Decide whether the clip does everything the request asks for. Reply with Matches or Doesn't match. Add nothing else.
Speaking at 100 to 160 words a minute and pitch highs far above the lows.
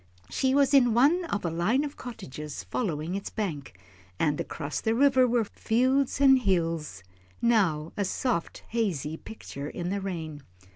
Matches